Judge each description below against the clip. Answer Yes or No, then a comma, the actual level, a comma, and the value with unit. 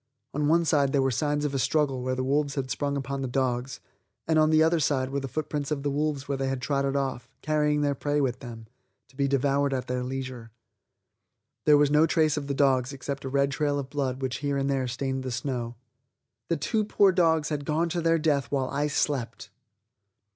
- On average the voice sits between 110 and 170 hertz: Yes, medium, 140 Hz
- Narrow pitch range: Yes, narrow, 2.1 semitones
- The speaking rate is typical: No, fast, 220 wpm